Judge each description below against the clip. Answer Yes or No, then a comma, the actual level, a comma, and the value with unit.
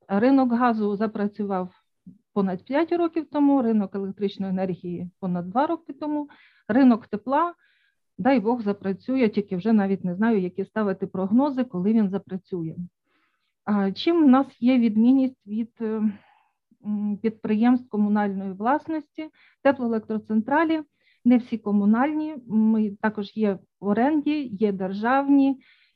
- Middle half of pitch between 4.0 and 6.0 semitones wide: Yes, average, 5.2 semitones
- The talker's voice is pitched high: Yes, high, 220 Hz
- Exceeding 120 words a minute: No, average, 115 wpm